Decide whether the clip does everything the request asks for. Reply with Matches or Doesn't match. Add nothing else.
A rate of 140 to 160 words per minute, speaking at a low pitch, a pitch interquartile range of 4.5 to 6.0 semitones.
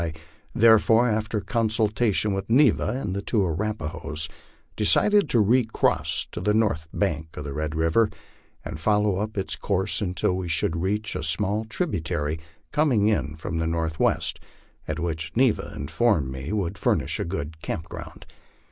Matches